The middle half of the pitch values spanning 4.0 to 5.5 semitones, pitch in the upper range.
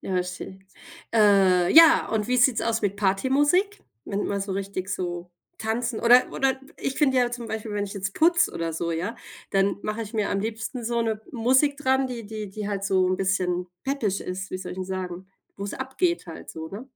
Yes: average, 4.6 semitones; high, 210 Hz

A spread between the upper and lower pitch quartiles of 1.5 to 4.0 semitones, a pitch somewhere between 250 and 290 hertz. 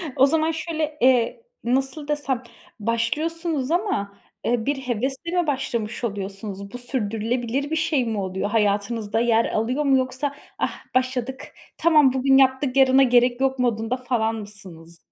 Yes: average, 3.6 semitones; very high, 255 Hz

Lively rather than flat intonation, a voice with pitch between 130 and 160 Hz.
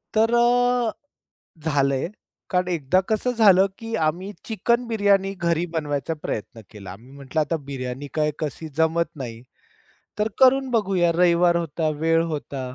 No: wide, 6.6 semitones; medium, 170 Hz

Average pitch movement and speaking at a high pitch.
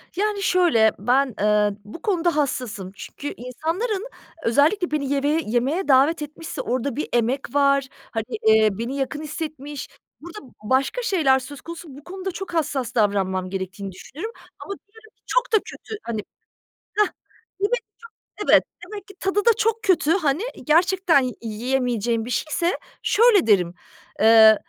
No: wide, 7.3 semitones; very high, 280 Hz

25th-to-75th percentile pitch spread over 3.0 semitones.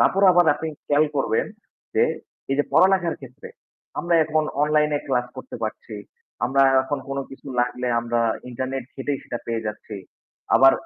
Yes: average, 3.6 semitones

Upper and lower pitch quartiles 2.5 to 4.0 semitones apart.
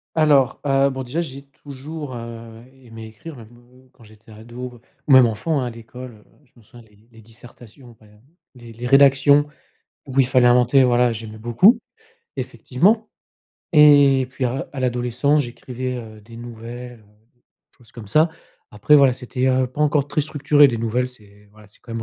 Yes: average, 3.0 semitones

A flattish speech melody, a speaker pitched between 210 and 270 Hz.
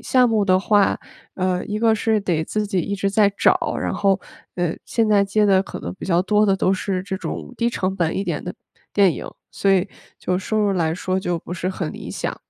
No: narrow, 2.2 semitones; high, 195 Hz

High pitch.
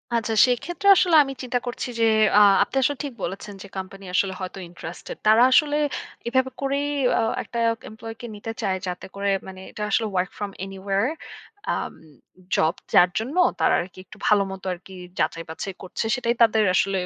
Yes: high, 210 Hz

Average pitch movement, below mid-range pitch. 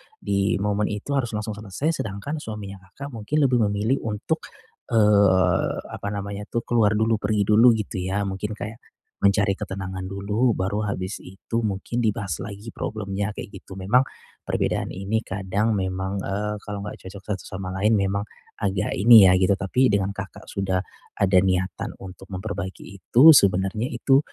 No: narrow, 2.2 semitones; low, 100 Hz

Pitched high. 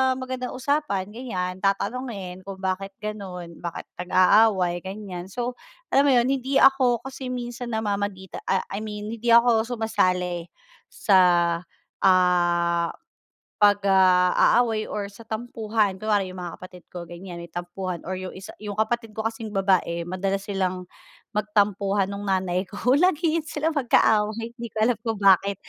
Yes: high, 205 Hz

